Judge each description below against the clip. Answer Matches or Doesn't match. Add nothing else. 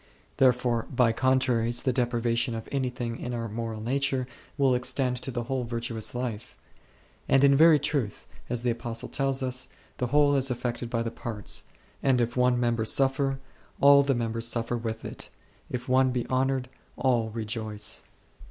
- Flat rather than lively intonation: Matches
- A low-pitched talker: Matches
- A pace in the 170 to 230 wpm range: Matches